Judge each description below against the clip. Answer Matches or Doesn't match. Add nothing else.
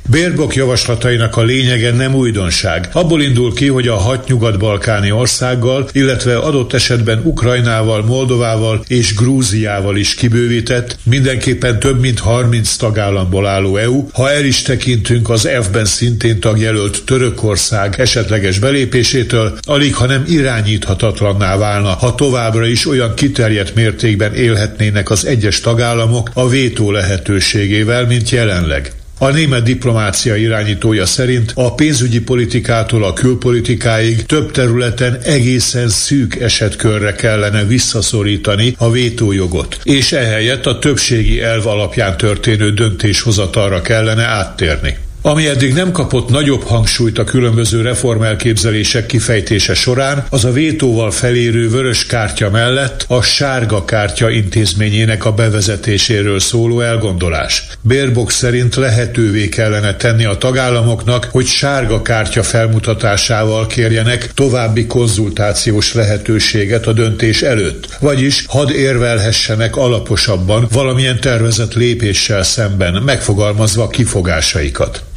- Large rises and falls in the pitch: Doesn't match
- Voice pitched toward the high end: Doesn't match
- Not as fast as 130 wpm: Matches